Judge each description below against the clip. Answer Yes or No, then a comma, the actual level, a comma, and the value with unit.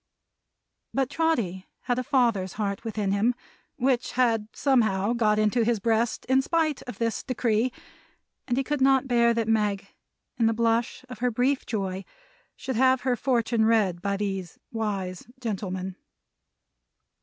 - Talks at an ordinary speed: Yes, average, 150 wpm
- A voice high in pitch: Yes, high, 230 Hz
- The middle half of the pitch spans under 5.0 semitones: Yes, average, 3.6 semitones